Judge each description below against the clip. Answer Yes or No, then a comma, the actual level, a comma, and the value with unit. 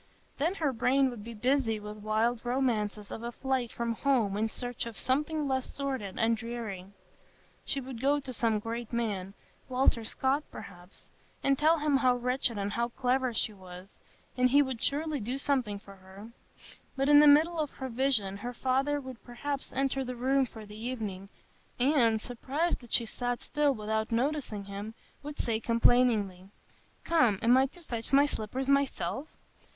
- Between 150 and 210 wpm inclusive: Yes, average, 170 wpm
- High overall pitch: Yes, high, 245 Hz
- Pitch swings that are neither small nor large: Yes, average, 3.9 semitones